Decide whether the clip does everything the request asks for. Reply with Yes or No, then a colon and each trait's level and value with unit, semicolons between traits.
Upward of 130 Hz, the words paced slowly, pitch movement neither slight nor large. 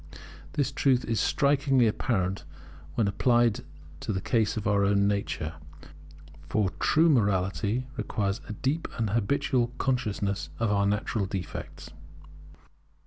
No: low, 110 Hz; slow, 125 wpm; average, 4.1 semitones